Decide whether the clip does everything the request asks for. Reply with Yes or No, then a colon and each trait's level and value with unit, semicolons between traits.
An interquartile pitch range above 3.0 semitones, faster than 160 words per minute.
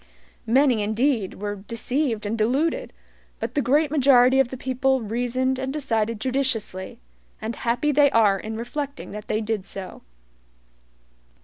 No: average, 3.6 semitones; average, 140 wpm